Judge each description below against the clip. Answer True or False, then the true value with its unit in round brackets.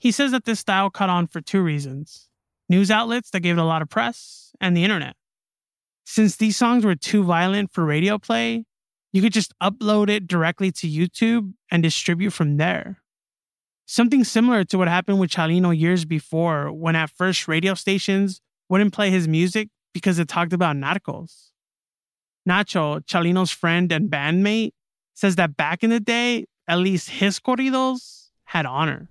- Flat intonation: False (3.8 semitones)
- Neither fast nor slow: True (170 wpm)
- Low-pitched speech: False (185 Hz)